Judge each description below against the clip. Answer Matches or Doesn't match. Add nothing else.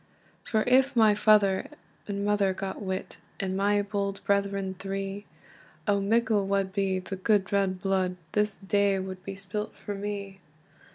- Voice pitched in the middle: Doesn't match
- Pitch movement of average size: Doesn't match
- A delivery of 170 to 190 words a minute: Doesn't match